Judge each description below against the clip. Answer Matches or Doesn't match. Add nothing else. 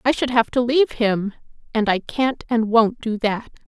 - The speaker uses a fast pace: Matches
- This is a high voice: Matches